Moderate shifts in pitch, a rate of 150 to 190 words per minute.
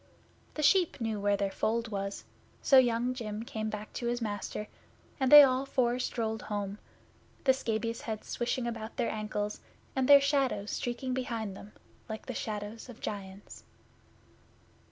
Yes: average, 3.3 semitones; average, 155 wpm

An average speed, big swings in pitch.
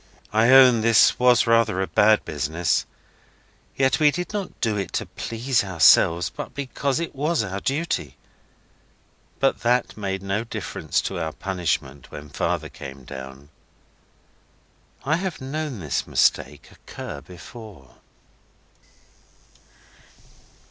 No: slow, 120 wpm; wide, 7.6 semitones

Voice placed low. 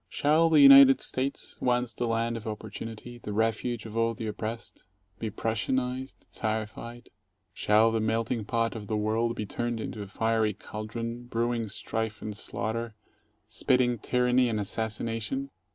Yes: low, 115 Hz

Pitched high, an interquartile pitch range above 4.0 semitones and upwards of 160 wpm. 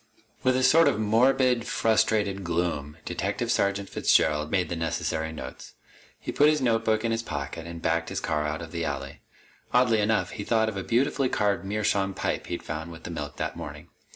No: low, 100 Hz; wide, 5.6 semitones; average, 195 wpm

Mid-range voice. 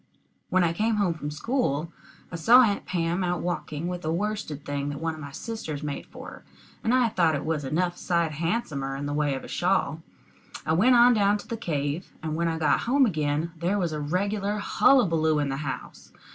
Yes: medium, 170 Hz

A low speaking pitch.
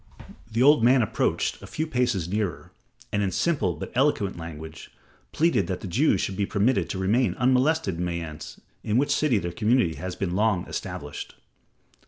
Yes: low, 105 Hz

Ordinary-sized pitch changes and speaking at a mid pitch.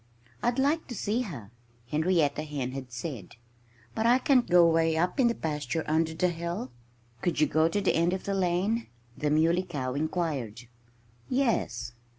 Yes: average, 4.8 semitones; medium, 165 Hz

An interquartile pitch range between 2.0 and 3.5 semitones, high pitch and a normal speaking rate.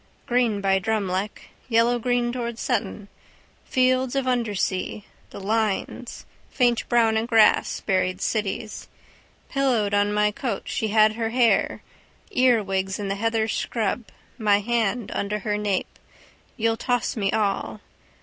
No: average, 2.8 semitones; high, 220 Hz; slow, 130 wpm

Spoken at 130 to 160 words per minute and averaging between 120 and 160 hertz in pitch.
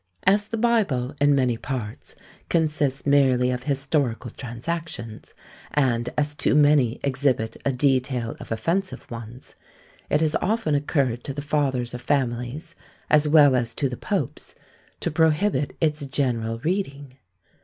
Yes: average, 140 wpm; medium, 140 Hz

